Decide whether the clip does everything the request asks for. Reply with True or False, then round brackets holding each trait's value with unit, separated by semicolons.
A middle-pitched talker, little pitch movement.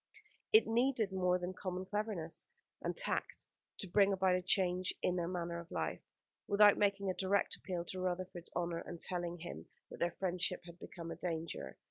True (180 Hz; 2.1 semitones)